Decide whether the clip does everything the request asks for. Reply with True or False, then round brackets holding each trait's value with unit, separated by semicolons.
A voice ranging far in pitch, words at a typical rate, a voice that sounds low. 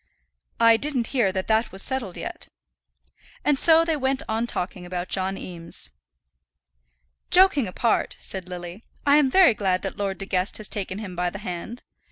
False (6.1 semitones; 175 wpm; 205 Hz)